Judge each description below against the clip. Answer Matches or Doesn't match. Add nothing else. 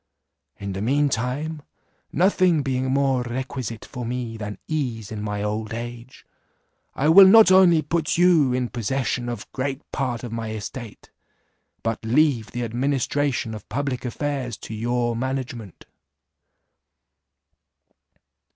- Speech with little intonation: Doesn't match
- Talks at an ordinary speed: Doesn't match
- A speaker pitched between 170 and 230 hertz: Doesn't match